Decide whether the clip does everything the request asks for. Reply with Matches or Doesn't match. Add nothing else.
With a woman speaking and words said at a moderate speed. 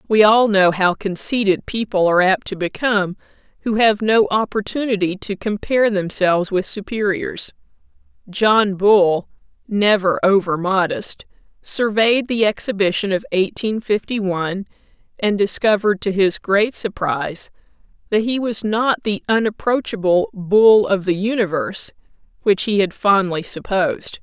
Doesn't match